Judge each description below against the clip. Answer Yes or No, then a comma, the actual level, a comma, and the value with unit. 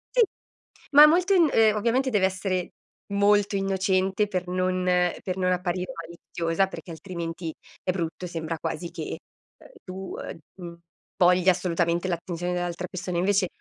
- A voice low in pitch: No, medium, 185 Hz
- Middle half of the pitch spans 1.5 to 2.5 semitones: Yes, narrow, 2.2 semitones